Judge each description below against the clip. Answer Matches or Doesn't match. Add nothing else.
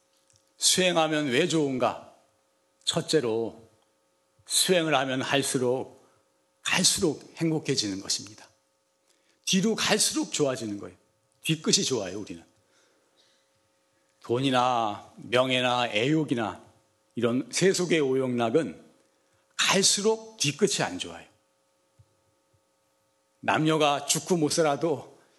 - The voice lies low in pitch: Matches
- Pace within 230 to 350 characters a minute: Doesn't match